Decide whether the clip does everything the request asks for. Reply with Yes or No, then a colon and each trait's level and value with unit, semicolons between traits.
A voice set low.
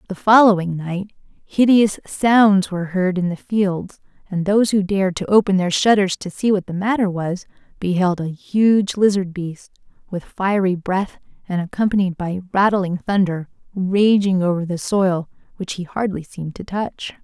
No: high, 190 Hz